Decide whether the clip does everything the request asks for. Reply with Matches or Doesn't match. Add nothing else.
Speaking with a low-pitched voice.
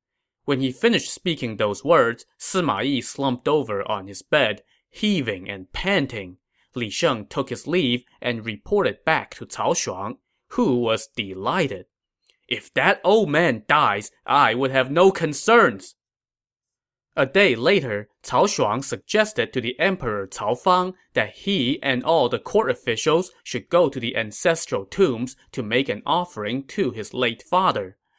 Matches